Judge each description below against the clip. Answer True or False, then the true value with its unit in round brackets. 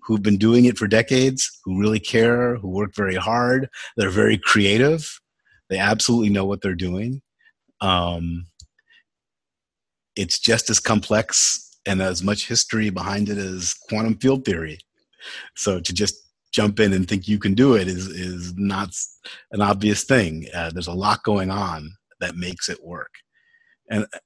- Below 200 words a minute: True (160 wpm)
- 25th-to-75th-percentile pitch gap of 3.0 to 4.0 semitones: True (3.5 semitones)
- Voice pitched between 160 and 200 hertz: False (100 Hz)